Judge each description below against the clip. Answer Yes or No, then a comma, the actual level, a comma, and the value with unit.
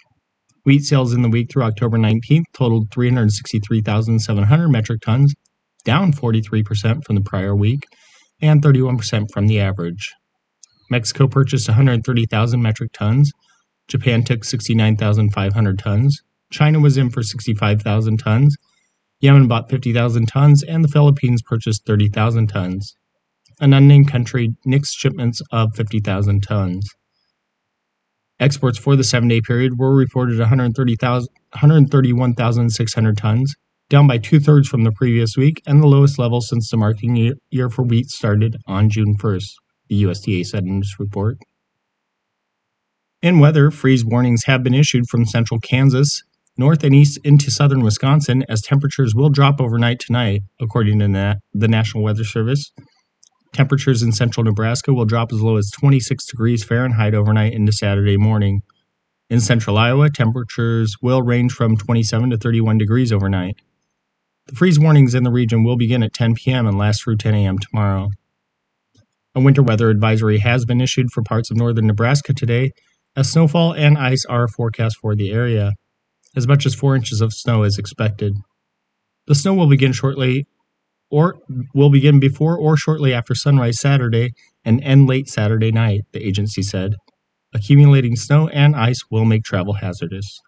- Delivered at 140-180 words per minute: Yes, average, 150 wpm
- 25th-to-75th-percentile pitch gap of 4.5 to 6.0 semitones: No, average, 3.7 semitones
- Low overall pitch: Yes, low, 120 Hz